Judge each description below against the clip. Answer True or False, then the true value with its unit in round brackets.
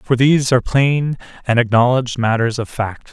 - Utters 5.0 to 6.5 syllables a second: True (5.5 syllables/s)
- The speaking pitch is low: True (125 Hz)